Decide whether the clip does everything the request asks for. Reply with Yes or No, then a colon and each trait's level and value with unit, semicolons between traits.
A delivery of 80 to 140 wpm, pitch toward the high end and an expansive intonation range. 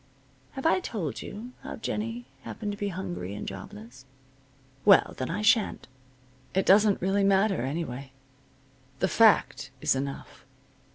Yes: slow, 135 wpm; high, 195 Hz; wide, 7.6 semitones